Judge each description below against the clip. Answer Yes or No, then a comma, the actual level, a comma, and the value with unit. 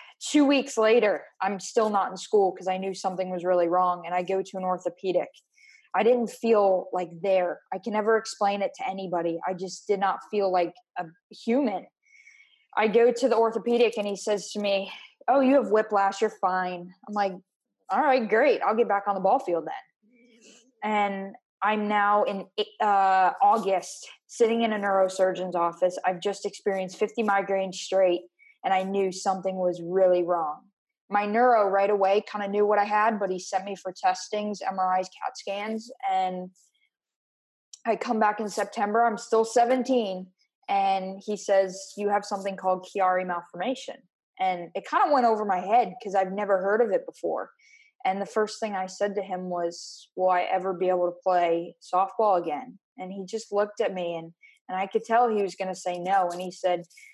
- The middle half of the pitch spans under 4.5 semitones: Yes, average, 3.6 semitones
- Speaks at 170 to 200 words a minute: Yes, average, 195 wpm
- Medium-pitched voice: No, high, 200 Hz